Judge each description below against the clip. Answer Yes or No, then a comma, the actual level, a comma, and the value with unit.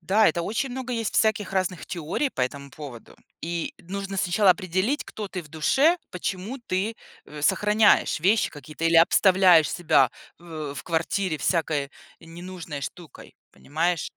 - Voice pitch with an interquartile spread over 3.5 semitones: Yes, average, 4.2 semitones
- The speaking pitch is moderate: Yes, medium, 180 Hz